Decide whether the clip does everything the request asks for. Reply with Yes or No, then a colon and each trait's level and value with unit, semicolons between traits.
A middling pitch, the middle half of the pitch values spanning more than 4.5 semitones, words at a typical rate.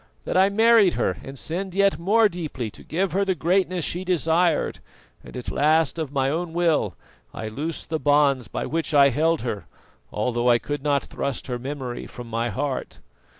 Yes: medium, 155 Hz; average, 5.0 semitones; average, 190 wpm